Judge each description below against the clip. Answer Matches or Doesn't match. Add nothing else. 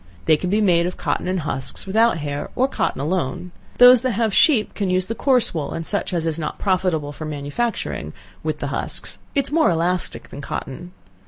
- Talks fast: Matches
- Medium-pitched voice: Matches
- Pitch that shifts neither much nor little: Doesn't match